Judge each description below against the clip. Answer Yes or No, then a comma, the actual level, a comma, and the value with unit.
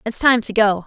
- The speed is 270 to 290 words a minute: Yes, fast, 280 wpm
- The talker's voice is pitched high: Yes, high, 220 Hz